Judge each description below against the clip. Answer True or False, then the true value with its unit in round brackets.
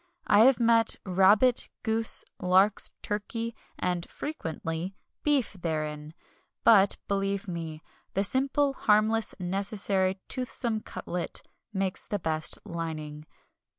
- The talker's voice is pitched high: True (195 Hz)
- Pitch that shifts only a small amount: False (4.8 semitones)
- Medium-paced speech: False (105 wpm)